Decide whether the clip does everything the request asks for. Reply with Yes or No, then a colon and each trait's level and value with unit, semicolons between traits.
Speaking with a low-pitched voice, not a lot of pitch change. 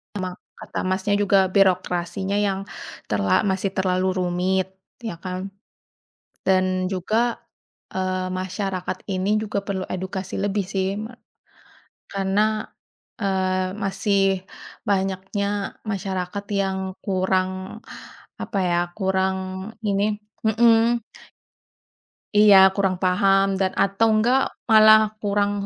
No: high, 195 Hz; narrow, 1.5 semitones